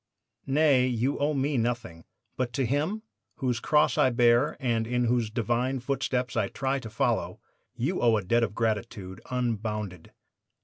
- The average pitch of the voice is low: Yes, low, 120 Hz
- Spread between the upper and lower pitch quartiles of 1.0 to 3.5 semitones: Yes, average, 3.0 semitones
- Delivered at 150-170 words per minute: Yes, average, 160 wpm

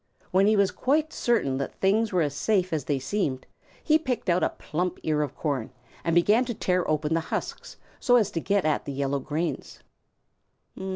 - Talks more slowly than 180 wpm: No, average, 195 wpm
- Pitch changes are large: Yes, wide, 5.9 semitones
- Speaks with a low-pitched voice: No, medium, 175 Hz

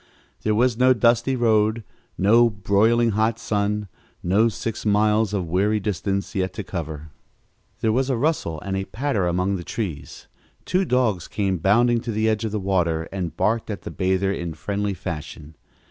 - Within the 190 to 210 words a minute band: No, average, 175 wpm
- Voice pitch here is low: Yes, low, 105 Hz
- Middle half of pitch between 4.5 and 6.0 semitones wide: No, average, 3.4 semitones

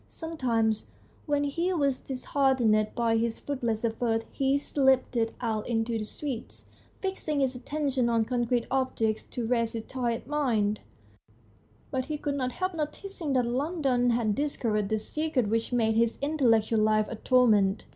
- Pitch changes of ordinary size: Yes, average, 3.8 semitones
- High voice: Yes, high, 245 Hz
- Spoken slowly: No, average, 155 wpm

